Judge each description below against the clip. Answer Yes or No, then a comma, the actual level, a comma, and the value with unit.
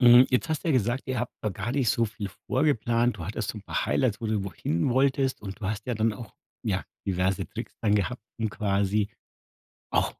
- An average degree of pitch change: Yes, average, 3.6 semitones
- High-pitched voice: No, low, 110 Hz